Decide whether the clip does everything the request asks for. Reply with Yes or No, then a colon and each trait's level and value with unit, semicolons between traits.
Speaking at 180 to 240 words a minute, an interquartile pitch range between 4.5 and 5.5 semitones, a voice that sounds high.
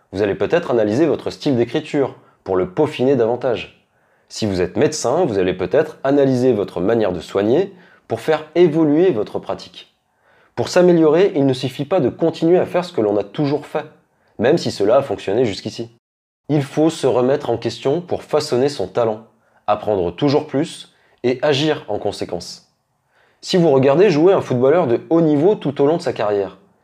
No: average, 185 wpm; average, 5.1 semitones; medium, 140 Hz